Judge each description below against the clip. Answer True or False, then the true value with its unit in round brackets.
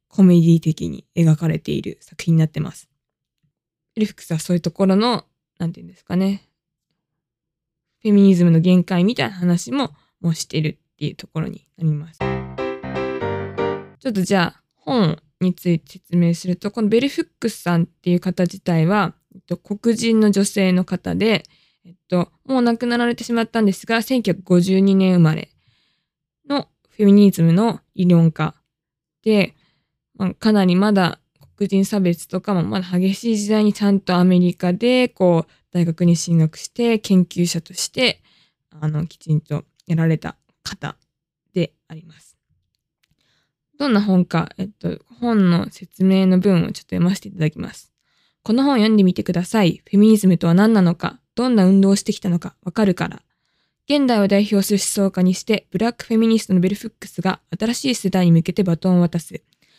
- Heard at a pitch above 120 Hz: True (185 Hz)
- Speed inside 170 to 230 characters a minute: False (335 characters per minute)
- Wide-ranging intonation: False (3.7 semitones)